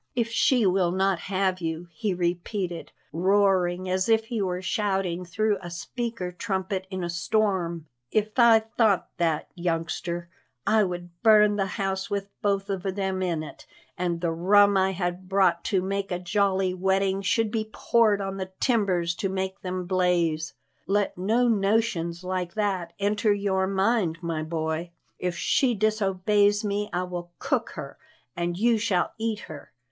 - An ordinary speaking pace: Yes, average, 160 wpm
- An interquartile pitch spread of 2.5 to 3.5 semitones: Yes, average, 2.8 semitones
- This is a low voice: No, high, 190 Hz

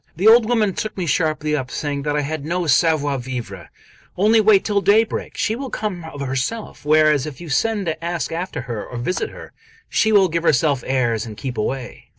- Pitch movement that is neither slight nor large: No, wide, 6.5 semitones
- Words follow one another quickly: Yes, fast, 210 wpm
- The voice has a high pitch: No, medium, 155 Hz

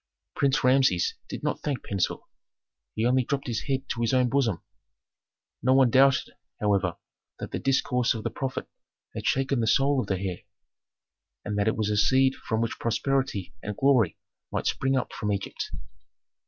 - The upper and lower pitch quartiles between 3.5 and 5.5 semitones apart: Yes, average, 4.3 semitones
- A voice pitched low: Yes, low, 125 Hz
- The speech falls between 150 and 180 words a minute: Yes, average, 175 wpm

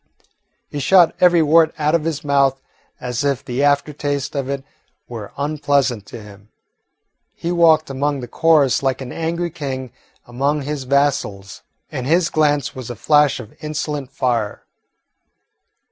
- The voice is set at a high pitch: No, medium, 140 Hz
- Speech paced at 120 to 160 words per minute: Yes, average, 150 wpm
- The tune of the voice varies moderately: Yes, average, 3.0 semitones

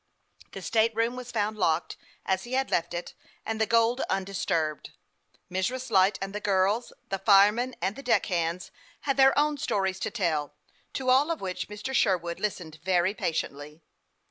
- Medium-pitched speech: No, high, 200 Hz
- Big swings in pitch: No, average, 4.7 semitones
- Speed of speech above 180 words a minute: No, average, 175 wpm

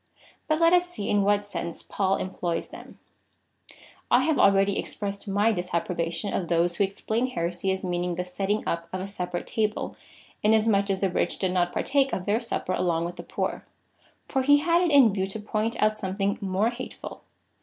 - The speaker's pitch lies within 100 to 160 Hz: No, high, 200 Hz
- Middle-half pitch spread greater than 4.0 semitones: No, average, 3.5 semitones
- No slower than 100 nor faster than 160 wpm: No, average, 195 wpm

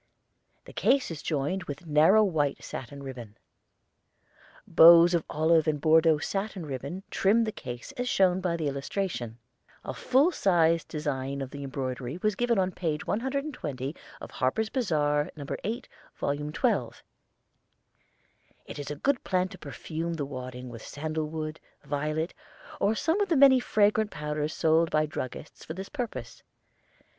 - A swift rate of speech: No, average, 150 wpm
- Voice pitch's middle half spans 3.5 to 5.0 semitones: No, wide, 5.4 semitones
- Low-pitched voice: No, medium, 160 Hz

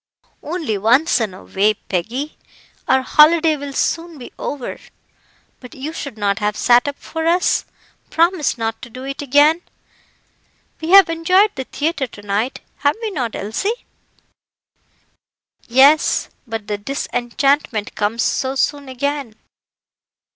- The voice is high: Yes, very high, 275 Hz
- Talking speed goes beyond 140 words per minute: No, slow, 135 wpm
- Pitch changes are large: Yes, wide, 5.8 semitones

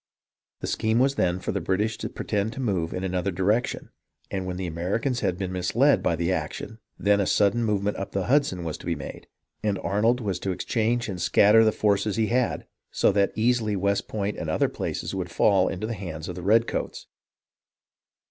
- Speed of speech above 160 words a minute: Yes, fast, 205 wpm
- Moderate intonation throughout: Yes, average, 3.3 semitones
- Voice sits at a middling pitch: No, low, 100 Hz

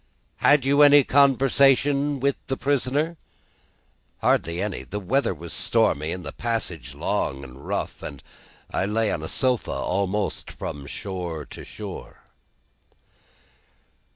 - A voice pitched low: Yes, low, 115 Hz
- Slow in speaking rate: Yes, slow, 125 wpm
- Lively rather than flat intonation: Yes, wide, 8.2 semitones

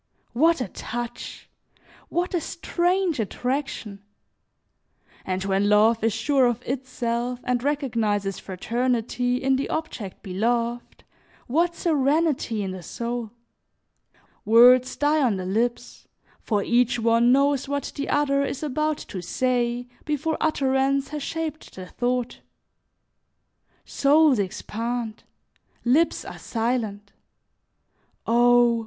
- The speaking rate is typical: No, slow, 110 wpm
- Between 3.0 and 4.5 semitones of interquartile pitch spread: Yes, average, 3.7 semitones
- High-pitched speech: Yes, high, 245 Hz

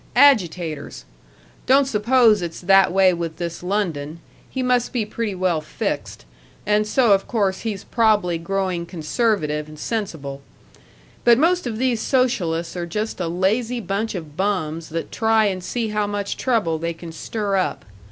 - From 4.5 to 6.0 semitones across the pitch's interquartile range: Yes, average, 4.9 semitones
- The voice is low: No, high, 195 Hz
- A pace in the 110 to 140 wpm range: No, average, 160 wpm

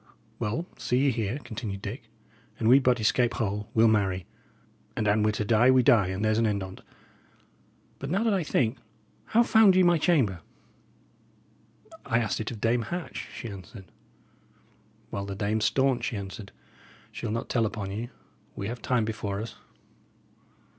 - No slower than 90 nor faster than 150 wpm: No, average, 170 wpm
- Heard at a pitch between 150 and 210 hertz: No, low, 110 Hz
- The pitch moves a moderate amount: Yes, average, 3.6 semitones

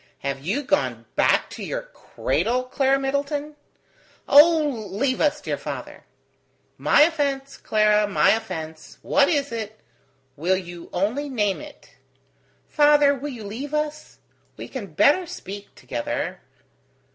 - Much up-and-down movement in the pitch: Yes, wide, 5.9 semitones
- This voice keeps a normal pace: No, slow, 130 wpm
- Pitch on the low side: No, very high, 270 Hz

